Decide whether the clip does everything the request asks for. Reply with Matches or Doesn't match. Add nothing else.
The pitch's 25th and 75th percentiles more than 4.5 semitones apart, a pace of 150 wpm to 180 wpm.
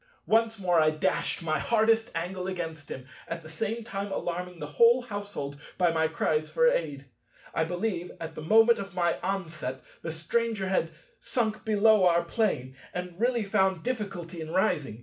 Matches